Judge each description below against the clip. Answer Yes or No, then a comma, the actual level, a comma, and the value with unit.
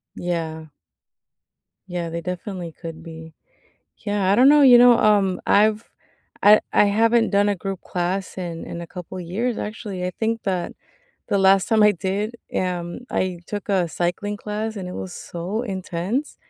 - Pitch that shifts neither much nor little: Yes, average, 3.3 semitones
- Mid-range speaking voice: No, high, 195 Hz